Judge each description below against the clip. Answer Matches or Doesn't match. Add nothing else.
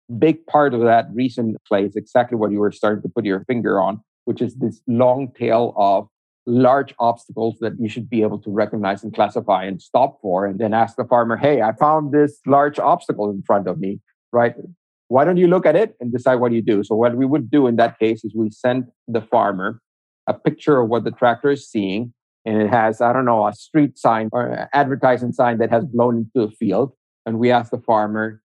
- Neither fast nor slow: Doesn't match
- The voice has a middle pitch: Doesn't match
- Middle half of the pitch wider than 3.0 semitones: Doesn't match